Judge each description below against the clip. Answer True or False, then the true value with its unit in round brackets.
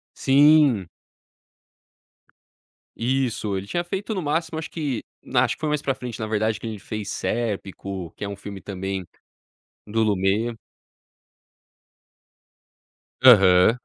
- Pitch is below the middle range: True (110 Hz)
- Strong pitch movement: True (6.0 semitones)